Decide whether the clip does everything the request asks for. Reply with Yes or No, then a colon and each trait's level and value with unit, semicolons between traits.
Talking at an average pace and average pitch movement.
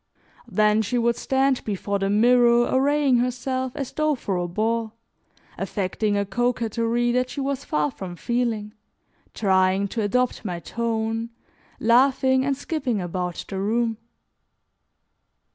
No: slow, 130 wpm; average, 3.6 semitones